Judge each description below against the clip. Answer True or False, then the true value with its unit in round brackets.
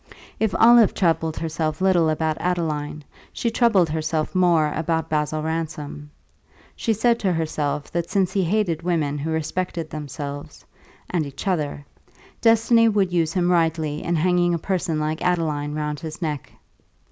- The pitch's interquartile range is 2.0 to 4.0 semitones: True (2.9 semitones)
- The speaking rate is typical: True (150 wpm)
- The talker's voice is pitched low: False (165 Hz)